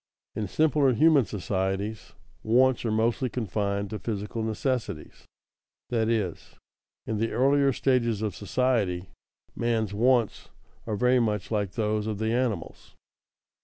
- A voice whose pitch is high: No, low, 110 Hz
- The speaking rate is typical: No, slow, 130 wpm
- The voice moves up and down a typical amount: Yes, average, 3.2 semitones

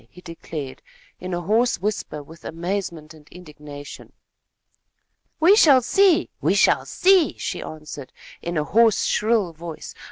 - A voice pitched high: No, medium, 175 Hz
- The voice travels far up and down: Yes, wide, 6.8 semitones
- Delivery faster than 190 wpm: No, slow, 135 wpm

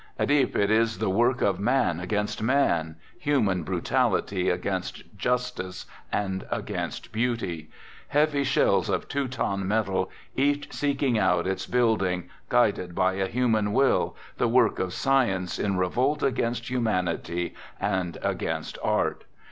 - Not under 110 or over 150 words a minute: Yes, average, 140 wpm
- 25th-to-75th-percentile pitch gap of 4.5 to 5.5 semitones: Yes, average, 5.2 semitones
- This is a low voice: Yes, low, 110 Hz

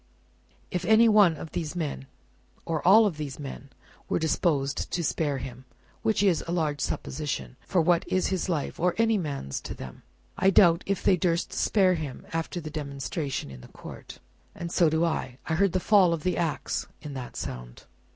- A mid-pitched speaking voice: Yes, medium, 165 Hz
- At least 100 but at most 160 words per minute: No, average, 190 wpm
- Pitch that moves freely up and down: No, average, 4.3 semitones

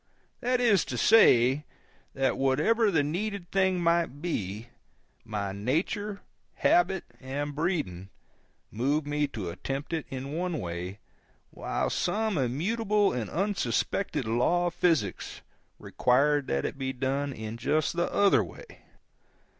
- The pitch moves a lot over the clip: Yes, wide, 6.4 semitones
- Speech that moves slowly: Yes, slow, 130 wpm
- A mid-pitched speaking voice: Yes, medium, 145 Hz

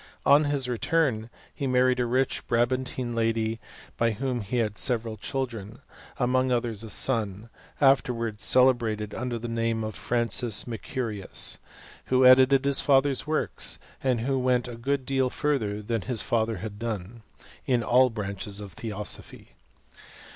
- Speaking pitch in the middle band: No, low, 120 Hz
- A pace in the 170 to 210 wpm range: No, average, 150 wpm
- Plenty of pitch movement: No, average, 2.7 semitones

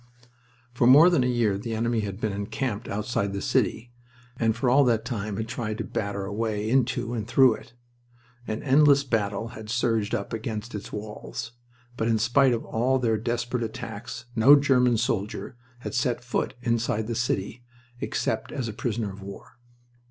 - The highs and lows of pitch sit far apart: No, narrow, 2.4 semitones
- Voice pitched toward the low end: Yes, low, 115 Hz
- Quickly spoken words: No, average, 180 wpm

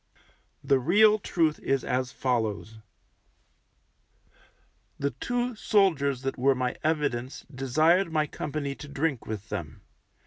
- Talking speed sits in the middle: No, slow, 115 wpm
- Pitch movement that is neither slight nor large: Yes, average, 4.2 semitones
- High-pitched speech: No, medium, 140 Hz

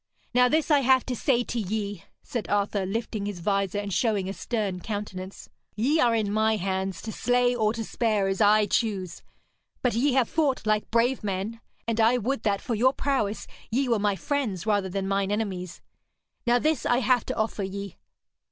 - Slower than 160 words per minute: No, average, 190 wpm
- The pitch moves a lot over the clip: No, average, 3.6 semitones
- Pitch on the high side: Yes, high, 215 Hz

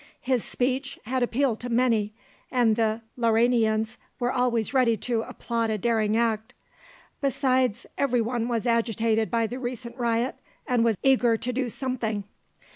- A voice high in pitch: Yes, high, 235 Hz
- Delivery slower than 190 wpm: Yes, average, 150 wpm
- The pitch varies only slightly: Yes, narrow, 2.0 semitones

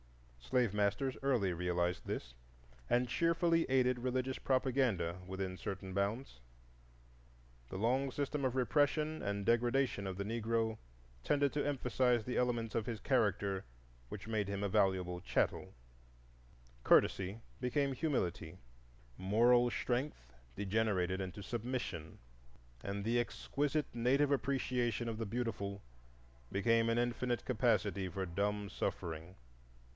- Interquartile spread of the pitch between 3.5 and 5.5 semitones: Yes, average, 4.7 semitones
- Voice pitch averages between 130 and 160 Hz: No, low, 115 Hz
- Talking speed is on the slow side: Yes, slow, 120 wpm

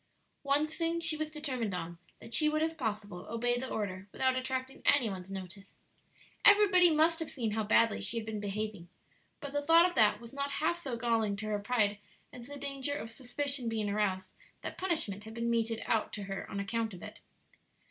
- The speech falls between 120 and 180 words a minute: No, fast, 205 wpm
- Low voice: No, high, 235 Hz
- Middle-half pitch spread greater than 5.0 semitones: Yes, wide, 5.6 semitones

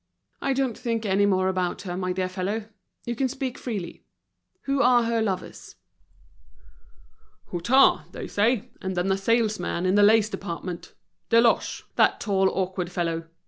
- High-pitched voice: Yes, high, 200 Hz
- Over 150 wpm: No, average, 145 wpm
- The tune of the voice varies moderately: Yes, average, 4.0 semitones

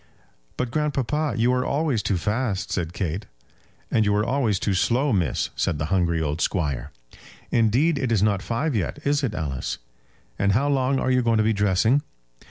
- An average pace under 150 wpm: No, average, 185 wpm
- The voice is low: Yes, low, 110 Hz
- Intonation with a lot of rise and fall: Yes, wide, 5.8 semitones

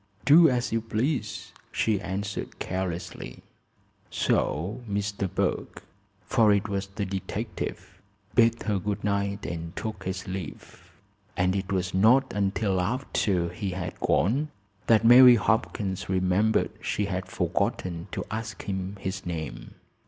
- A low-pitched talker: Yes, low, 100 Hz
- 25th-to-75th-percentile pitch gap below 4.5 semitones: Yes, average, 2.9 semitones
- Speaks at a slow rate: Yes, slow, 130 wpm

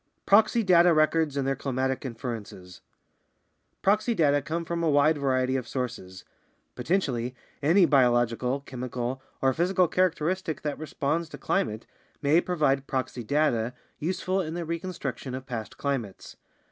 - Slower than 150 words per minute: Yes, average, 140 wpm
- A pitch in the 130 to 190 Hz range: Yes, medium, 140 Hz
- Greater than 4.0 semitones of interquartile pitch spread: Yes, average, 4.9 semitones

